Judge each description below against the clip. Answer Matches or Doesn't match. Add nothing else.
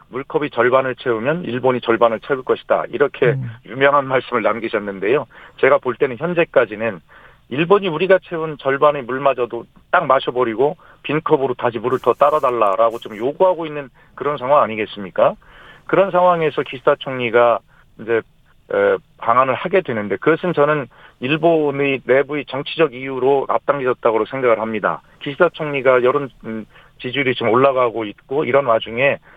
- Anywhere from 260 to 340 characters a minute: Doesn't match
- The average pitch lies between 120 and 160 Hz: Matches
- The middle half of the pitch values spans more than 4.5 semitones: Doesn't match